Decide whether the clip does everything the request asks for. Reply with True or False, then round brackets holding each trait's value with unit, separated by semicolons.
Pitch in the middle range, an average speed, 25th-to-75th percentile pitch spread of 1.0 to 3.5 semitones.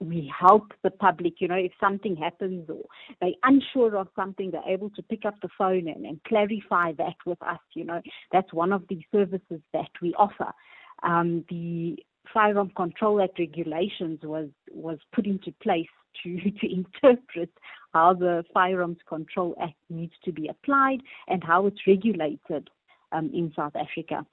True (180 Hz; 165 wpm; 3.1 semitones)